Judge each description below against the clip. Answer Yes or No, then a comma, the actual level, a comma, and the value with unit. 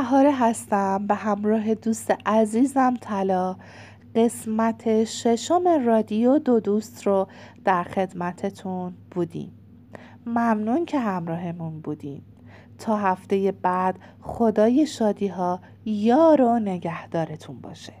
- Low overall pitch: No, high, 210 Hz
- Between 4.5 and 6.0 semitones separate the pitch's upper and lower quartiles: No, average, 4.1 semitones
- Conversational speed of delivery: No, slow, 100 wpm